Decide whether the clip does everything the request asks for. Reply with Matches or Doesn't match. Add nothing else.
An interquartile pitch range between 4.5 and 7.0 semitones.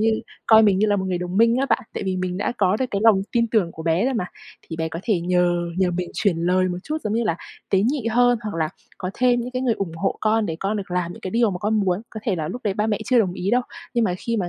Doesn't match